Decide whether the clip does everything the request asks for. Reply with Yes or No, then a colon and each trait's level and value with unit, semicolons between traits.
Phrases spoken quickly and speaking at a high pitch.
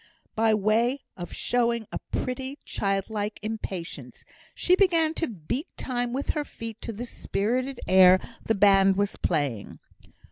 No: average, 140 wpm; high, 225 Hz